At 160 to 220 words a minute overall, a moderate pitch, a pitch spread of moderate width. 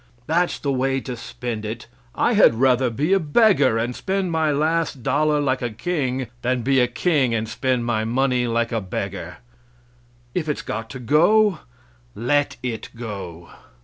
No: average, 170 wpm; low, 130 Hz; average, 4.5 semitones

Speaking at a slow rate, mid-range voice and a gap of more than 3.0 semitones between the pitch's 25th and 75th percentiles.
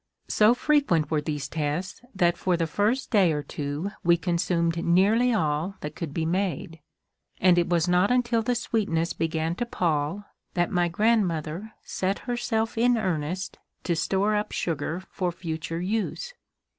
No: average, 155 wpm; medium, 175 Hz; average, 4.4 semitones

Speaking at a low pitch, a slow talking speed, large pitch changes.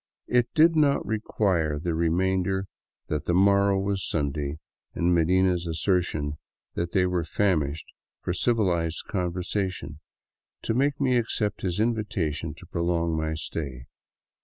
No: very low, 90 Hz; slow, 130 wpm; average, 3.7 semitones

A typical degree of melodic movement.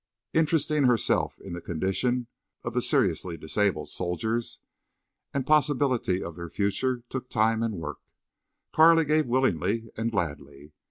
No: wide, 6.9 semitones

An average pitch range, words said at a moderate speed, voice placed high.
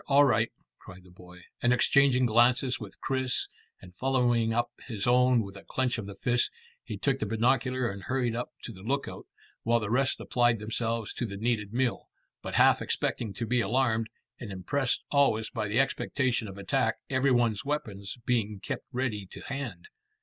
No: average, 3.3 semitones; average, 185 wpm; low, 120 Hz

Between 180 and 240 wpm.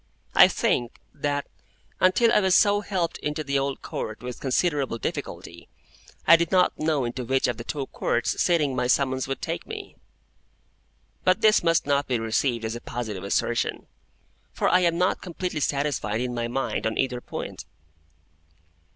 No: average, 170 wpm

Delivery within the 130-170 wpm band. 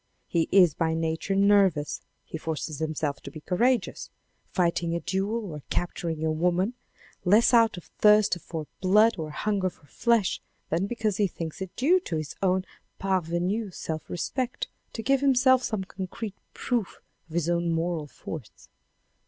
Yes: average, 160 wpm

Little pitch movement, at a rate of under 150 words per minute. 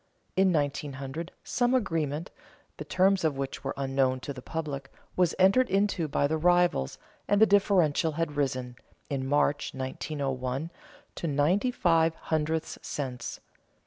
No: average, 4.5 semitones; average, 140 wpm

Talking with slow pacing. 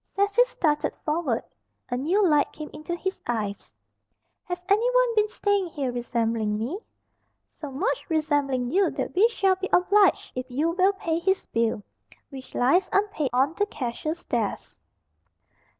No: average, 150 wpm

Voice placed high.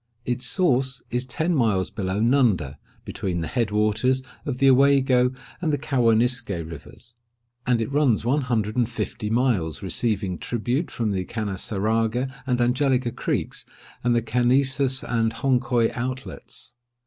No: low, 120 Hz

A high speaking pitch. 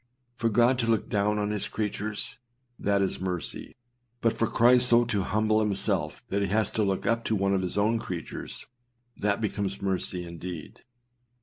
No: low, 105 Hz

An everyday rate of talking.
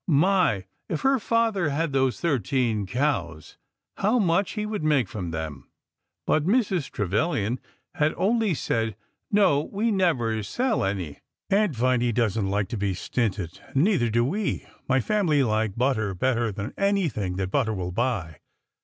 Yes: average, 155 wpm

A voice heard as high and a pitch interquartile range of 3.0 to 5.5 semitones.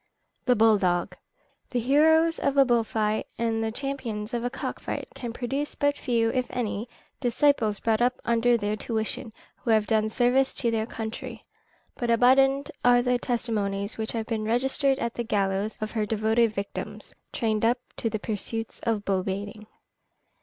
No: high, 230 Hz; narrow, 2.5 semitones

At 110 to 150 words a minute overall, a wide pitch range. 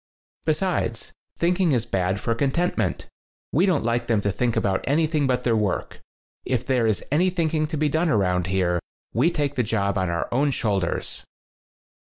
No: average, 180 wpm; wide, 7.2 semitones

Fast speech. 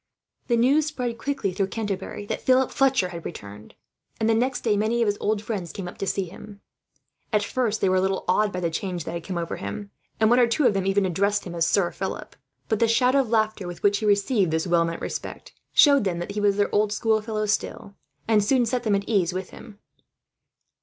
Yes: fast, 240 wpm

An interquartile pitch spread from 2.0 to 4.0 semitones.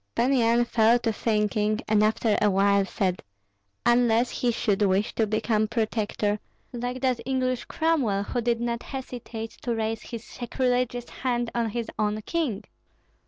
Yes: narrow, 2.4 semitones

